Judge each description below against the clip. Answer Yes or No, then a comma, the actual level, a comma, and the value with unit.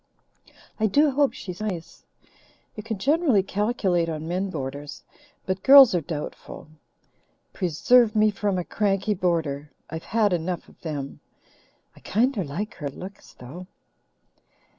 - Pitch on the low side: No, medium, 185 Hz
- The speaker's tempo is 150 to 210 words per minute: No, slow, 135 wpm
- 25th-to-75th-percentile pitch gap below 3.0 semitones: No, average, 4.7 semitones